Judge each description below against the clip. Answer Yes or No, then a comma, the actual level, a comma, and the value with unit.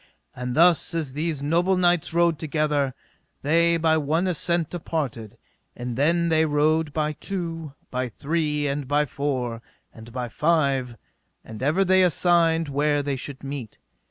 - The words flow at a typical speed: Yes, average, 150 wpm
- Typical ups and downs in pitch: Yes, average, 3.3 semitones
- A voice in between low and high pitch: Yes, medium, 150 Hz